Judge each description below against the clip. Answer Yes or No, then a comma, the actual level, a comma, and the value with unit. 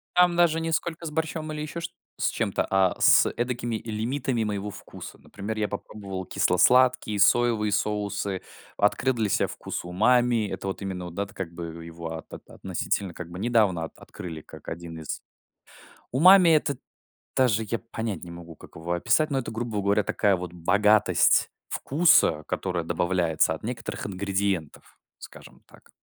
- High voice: No, low, 105 Hz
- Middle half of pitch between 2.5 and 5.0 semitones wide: No, wide, 5.4 semitones